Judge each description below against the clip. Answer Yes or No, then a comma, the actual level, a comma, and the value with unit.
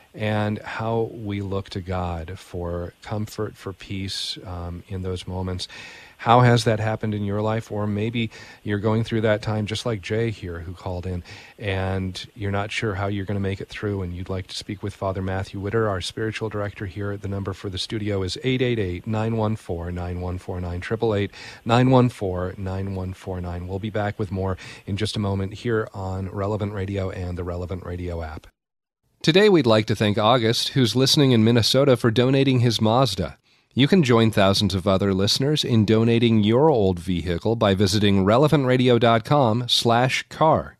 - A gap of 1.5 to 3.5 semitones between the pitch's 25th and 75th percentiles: Yes, average, 3.1 semitones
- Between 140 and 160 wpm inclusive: No, average, 170 wpm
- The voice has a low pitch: Yes, low, 105 Hz